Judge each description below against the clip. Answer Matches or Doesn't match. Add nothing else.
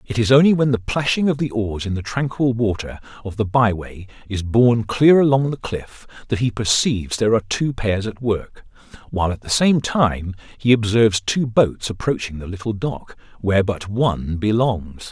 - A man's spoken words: Matches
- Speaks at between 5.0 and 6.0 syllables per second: Matches